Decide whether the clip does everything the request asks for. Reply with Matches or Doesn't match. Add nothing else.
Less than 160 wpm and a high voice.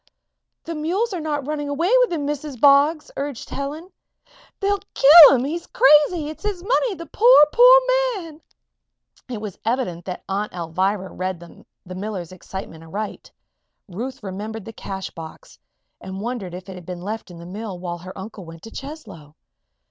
Doesn't match